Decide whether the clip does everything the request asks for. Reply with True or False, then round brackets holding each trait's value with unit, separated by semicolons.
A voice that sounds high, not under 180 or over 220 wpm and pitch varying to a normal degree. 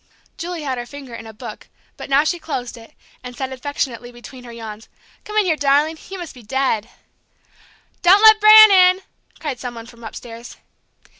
False (270 Hz; 190 wpm; 6.3 semitones)